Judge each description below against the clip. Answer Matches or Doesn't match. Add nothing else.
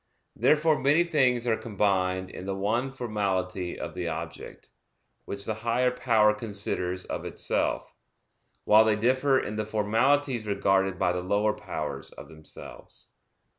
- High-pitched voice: Doesn't match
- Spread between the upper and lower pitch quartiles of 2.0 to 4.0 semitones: Doesn't match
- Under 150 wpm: Matches